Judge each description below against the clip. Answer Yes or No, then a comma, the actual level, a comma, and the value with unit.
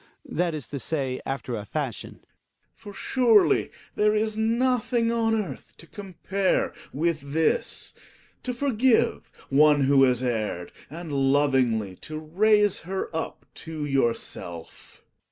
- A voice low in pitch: No, medium, 160 Hz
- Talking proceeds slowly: Yes, slow, 130 wpm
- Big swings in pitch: Yes, wide, 7.9 semitones